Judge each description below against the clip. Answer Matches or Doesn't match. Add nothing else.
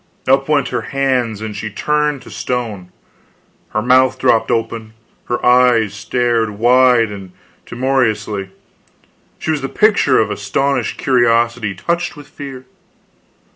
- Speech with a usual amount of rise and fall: Matches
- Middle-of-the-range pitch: Doesn't match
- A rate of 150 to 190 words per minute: Doesn't match